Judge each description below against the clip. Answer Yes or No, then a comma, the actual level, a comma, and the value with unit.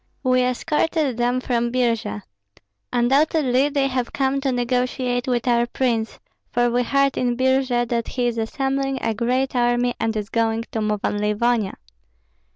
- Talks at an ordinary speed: Yes, average, 160 wpm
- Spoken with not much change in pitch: Yes, narrow, 1.9 semitones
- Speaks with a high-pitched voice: Yes, high, 245 Hz